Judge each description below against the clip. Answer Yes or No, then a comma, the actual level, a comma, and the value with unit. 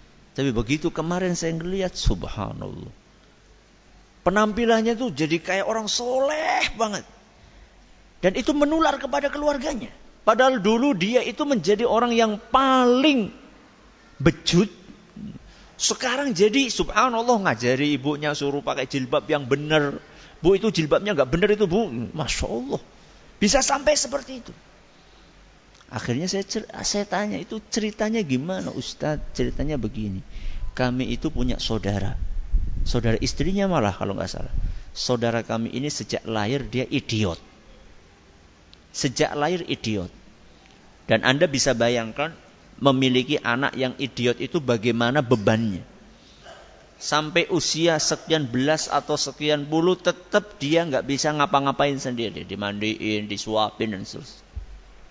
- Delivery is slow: No, average, 120 wpm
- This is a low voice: No, medium, 150 Hz